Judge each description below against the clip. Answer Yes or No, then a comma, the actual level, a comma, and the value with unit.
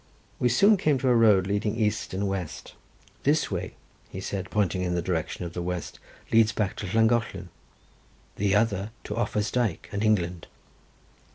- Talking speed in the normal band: Yes, average, 170 wpm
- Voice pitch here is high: No, low, 100 Hz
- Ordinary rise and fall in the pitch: Yes, average, 3.6 semitones